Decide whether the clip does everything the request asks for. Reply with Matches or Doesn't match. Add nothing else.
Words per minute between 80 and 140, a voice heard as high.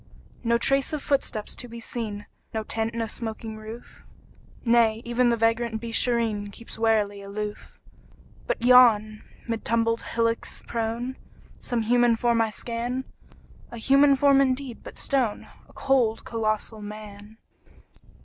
Matches